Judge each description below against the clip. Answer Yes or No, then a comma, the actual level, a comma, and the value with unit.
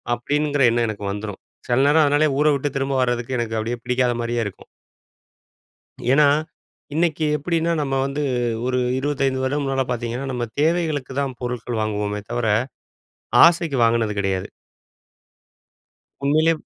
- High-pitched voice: No, low, 130 Hz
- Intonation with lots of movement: No, average, 3.7 semitones